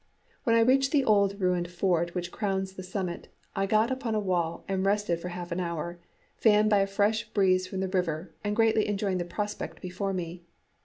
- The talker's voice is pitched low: No, high, 190 Hz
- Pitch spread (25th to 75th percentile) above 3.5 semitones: No, average, 2.8 semitones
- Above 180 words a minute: Yes, fast, 205 wpm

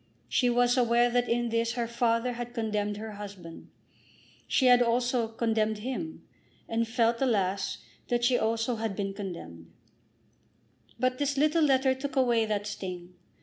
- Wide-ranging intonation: No, average, 2.8 semitones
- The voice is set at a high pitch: Yes, high, 230 Hz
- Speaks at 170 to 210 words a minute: No, average, 150 wpm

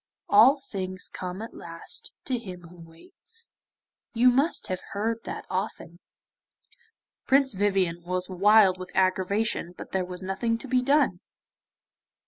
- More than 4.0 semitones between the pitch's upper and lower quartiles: Yes, average, 4.5 semitones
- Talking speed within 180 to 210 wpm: No, slow, 135 wpm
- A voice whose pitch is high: Yes, high, 195 Hz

